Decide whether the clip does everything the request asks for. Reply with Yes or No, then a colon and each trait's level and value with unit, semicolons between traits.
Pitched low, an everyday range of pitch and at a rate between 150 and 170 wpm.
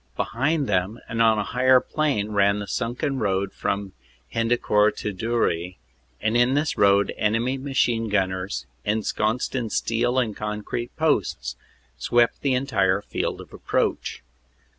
No: low, 115 Hz; average, 3.7 semitones; average, 140 wpm